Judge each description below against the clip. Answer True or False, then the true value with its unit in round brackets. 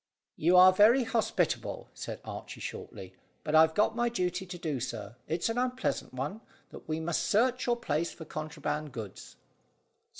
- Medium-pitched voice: True (175 Hz)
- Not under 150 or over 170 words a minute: True (165 wpm)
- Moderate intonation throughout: False (6.7 semitones)